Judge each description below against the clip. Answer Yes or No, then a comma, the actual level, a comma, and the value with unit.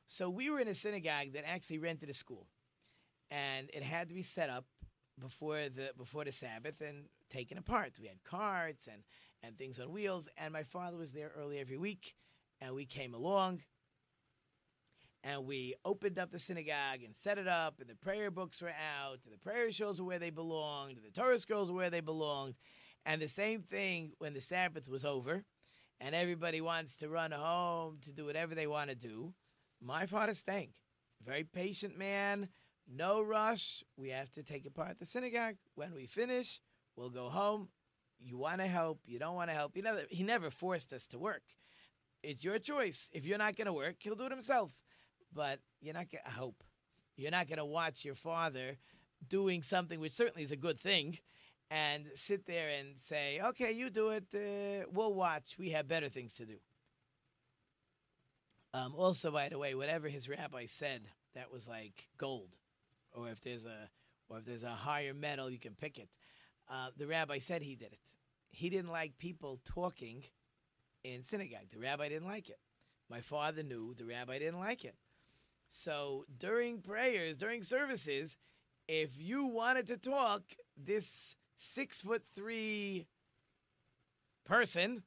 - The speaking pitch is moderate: Yes, medium, 155 Hz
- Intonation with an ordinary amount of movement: No, wide, 5.9 semitones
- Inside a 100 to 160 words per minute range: No, average, 185 wpm